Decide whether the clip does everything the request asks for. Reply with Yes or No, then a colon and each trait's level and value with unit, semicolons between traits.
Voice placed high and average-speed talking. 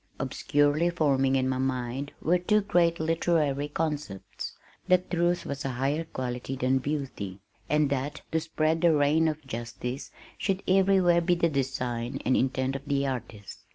No: medium, 145 Hz; average, 155 wpm